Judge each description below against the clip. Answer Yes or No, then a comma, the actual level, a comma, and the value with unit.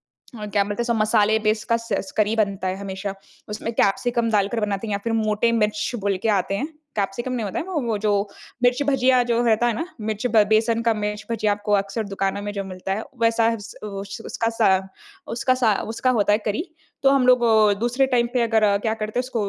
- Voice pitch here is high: Yes, high, 220 Hz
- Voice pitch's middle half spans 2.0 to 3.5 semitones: Yes, narrow, 2.5 semitones